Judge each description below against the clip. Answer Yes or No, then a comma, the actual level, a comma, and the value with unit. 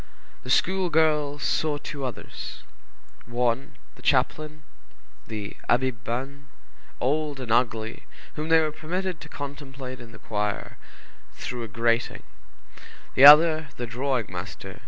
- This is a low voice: Yes, low, 130 Hz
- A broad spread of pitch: No, average, 4.5 semitones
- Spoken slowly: Yes, slow, 130 wpm